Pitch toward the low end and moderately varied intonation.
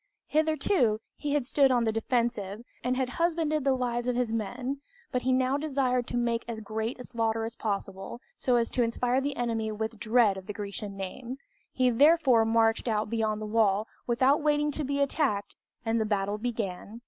No: high, 235 Hz; average, 3.1 semitones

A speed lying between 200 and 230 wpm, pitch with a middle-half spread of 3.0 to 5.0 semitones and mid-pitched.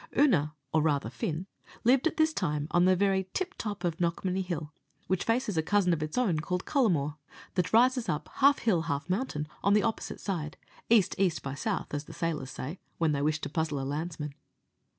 No: fast, 205 wpm; wide, 5.4 semitones; medium, 175 Hz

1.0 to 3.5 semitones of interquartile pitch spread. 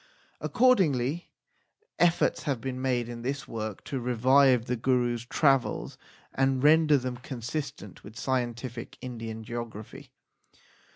Yes: narrow, 2.6 semitones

